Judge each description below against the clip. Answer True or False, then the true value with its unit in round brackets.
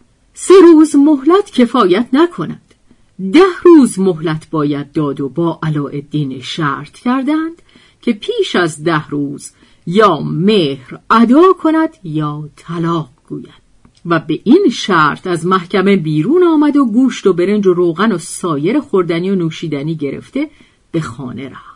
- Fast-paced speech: False (140 wpm)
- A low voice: False (185 Hz)